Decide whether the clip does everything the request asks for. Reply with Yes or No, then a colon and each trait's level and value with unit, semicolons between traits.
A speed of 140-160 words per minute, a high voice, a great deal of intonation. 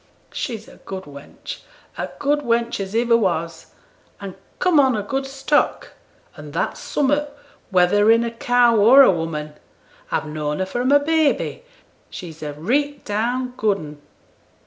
Yes: average, 155 wpm; high, 230 Hz; wide, 7.2 semitones